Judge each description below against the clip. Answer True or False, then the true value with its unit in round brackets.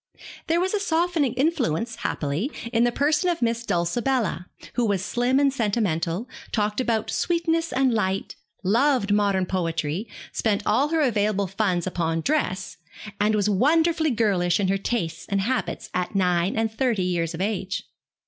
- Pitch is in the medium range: False (215 Hz)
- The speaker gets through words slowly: False (160 wpm)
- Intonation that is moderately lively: False (6.0 semitones)